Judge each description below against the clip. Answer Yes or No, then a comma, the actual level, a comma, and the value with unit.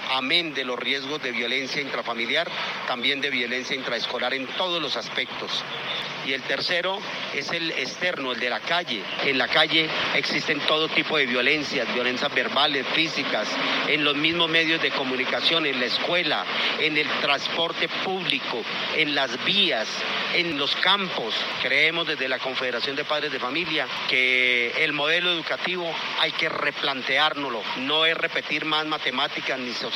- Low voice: No, medium, 150 Hz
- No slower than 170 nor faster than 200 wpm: No, average, 155 wpm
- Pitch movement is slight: No, average, 3.7 semitones